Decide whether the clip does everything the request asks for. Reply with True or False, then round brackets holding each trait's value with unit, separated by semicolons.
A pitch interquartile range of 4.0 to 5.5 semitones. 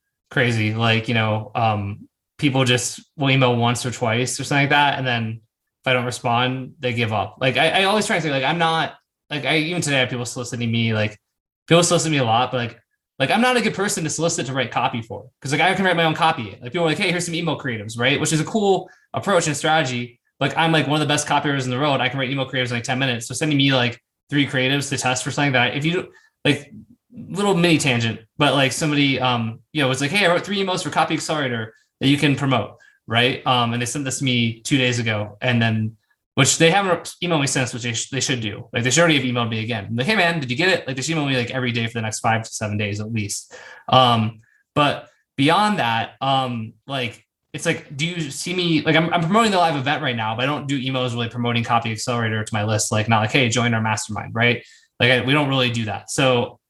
True (4.7 semitones)